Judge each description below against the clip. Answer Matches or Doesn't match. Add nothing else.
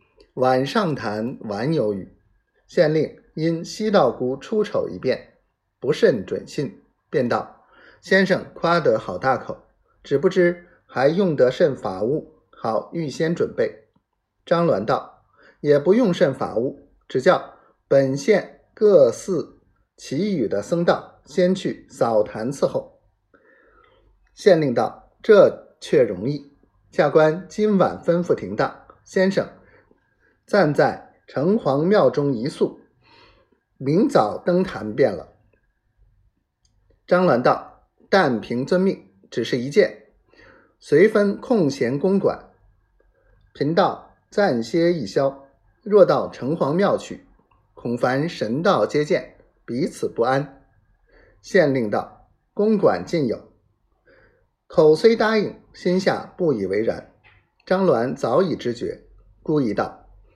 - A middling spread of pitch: Doesn't match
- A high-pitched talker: Doesn't match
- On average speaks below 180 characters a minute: Matches